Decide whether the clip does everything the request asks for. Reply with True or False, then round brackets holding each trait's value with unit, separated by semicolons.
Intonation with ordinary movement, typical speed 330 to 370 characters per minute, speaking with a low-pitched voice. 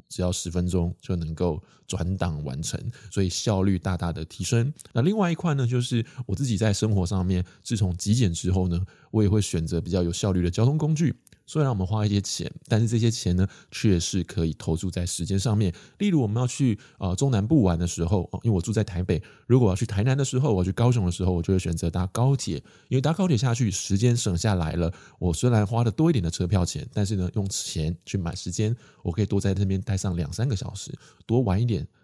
True (4.7 semitones; 345 characters per minute; 100 Hz)